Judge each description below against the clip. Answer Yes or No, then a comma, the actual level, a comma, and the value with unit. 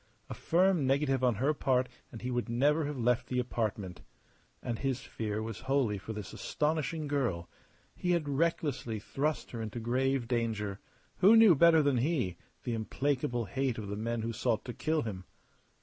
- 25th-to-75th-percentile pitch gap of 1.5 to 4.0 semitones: No, average, 4.4 semitones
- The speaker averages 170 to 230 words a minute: Yes, average, 180 wpm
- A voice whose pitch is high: No, low, 125 Hz